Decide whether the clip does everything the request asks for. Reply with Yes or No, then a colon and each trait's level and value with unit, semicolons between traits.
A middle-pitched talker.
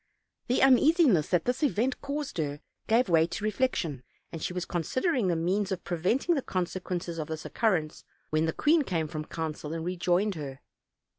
Yes: medium, 180 Hz